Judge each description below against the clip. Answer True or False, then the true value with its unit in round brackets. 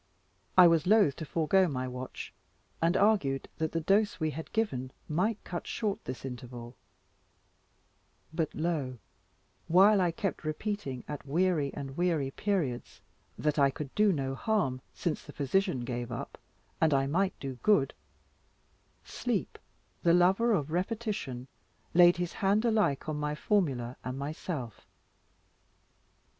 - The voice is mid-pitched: True (160 Hz)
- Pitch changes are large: True (6.0 semitones)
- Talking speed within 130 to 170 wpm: True (140 wpm)